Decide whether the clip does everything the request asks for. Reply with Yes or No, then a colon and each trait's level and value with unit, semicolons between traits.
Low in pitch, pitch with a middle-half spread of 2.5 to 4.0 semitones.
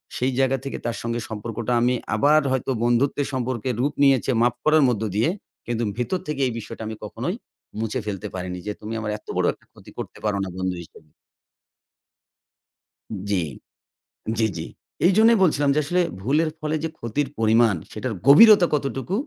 No: low, 120 Hz; average, 4.7 semitones